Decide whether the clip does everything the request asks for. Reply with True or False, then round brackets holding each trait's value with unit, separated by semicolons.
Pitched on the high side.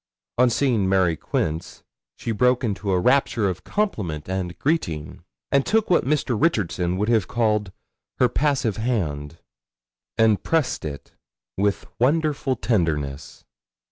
False (110 Hz)